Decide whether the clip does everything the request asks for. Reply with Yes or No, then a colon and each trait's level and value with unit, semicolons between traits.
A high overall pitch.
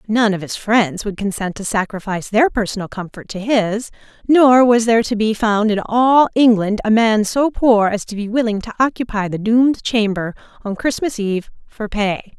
Yes: high, 220 Hz